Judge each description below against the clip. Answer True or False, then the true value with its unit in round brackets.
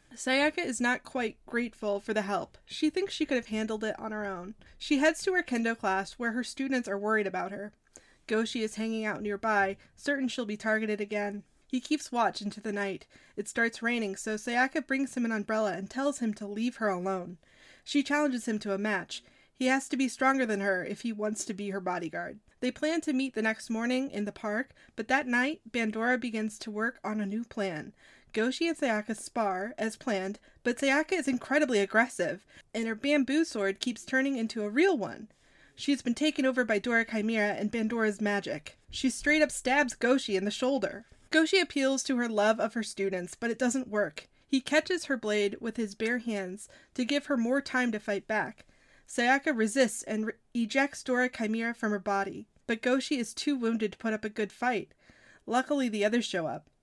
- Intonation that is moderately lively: True (3.9 semitones)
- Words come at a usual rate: False (210 wpm)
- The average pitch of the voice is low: False (230 Hz)